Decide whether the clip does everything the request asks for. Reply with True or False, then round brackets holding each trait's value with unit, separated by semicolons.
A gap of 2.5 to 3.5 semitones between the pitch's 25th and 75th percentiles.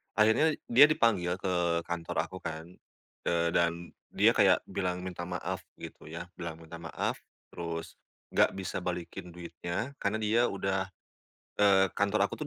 True (2.8 semitones)